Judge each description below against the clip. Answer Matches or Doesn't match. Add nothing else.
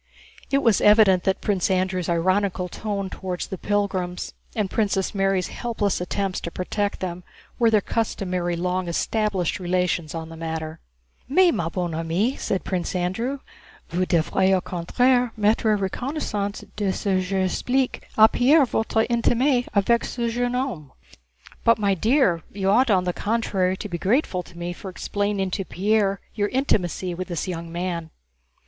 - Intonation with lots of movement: Doesn't match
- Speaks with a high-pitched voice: Matches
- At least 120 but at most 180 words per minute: Matches